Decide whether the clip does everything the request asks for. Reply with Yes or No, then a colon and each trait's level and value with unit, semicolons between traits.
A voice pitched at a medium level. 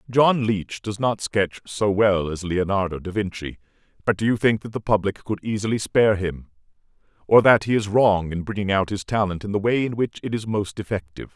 No: low, 105 Hz